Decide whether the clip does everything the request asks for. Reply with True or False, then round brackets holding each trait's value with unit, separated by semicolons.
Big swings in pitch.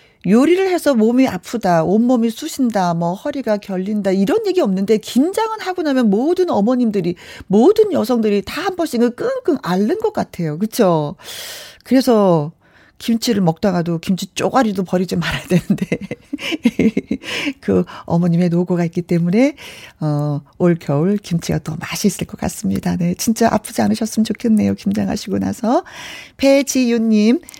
True (6.3 semitones)